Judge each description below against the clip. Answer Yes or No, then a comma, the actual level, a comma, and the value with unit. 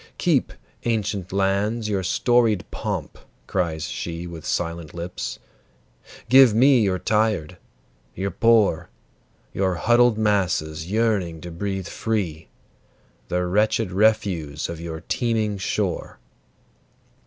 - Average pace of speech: No, slow, 110 wpm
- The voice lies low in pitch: Yes, very low, 95 Hz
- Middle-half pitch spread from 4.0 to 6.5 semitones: Yes, average, 4.4 semitones